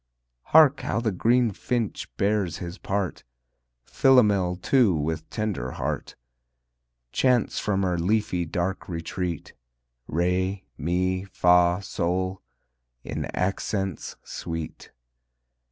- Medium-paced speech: No, slow, 100 wpm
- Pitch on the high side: No, very low, 95 Hz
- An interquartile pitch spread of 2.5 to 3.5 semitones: Yes, average, 3.2 semitones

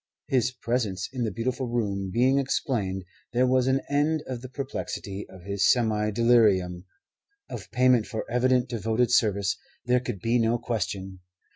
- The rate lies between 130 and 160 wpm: Yes, average, 155 wpm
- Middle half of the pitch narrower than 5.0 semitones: Yes, average, 4.0 semitones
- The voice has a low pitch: Yes, low, 120 Hz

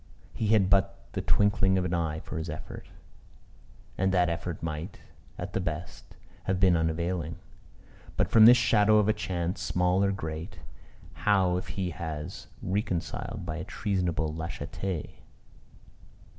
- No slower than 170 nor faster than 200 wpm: No, average, 145 wpm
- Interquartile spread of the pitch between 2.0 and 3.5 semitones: Yes, average, 3.0 semitones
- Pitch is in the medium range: No, very low, 90 Hz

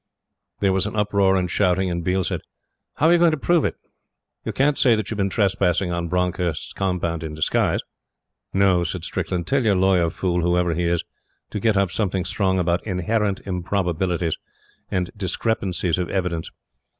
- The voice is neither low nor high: No, very low, 95 Hz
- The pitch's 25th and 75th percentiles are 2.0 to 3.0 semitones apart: Yes, narrow, 2.4 semitones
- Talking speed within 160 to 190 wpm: Yes, average, 175 wpm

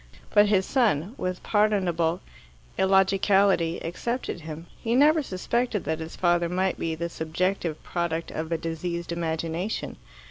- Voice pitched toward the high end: No, medium, 175 Hz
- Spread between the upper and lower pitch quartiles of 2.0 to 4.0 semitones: Yes, average, 3.3 semitones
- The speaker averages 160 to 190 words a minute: No, slow, 135 wpm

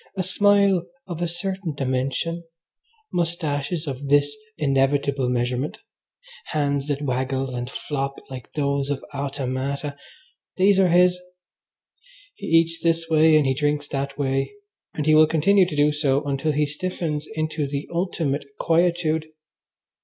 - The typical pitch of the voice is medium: Yes, medium, 150 Hz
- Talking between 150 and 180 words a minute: No, average, 140 wpm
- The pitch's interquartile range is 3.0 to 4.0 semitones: Yes, average, 3.3 semitones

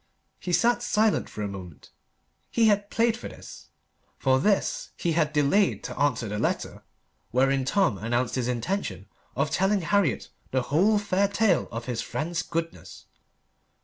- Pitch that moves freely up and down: Yes, wide, 8.0 semitones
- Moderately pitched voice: Yes, medium, 165 Hz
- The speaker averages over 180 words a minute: No, average, 155 wpm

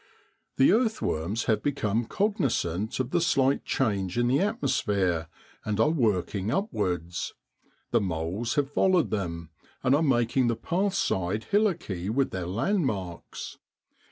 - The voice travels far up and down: Yes, wide, 7.8 semitones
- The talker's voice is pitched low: Yes, low, 115 Hz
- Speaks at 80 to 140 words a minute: Yes, slow, 135 wpm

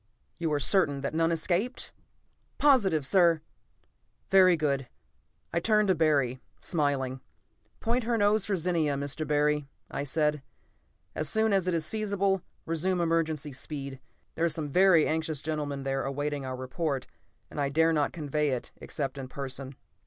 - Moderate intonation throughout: Yes, average, 4.3 semitones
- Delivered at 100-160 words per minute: Yes, average, 155 wpm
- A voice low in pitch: No, medium, 155 Hz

